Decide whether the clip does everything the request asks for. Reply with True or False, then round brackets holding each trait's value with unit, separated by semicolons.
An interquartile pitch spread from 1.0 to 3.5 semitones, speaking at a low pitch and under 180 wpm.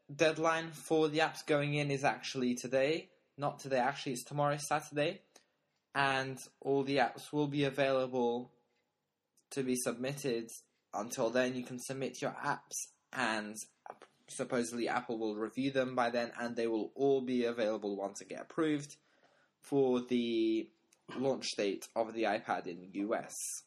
True (3.2 semitones; 130 Hz; 150 wpm)